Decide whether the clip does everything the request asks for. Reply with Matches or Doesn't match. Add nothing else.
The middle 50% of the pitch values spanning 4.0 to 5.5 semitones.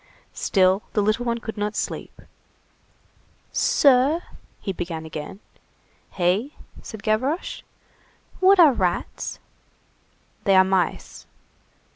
Matches